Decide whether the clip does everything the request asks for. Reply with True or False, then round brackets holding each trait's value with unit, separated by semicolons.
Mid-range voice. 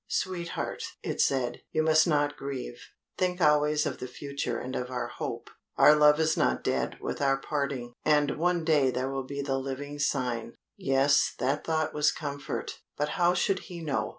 True (145 Hz)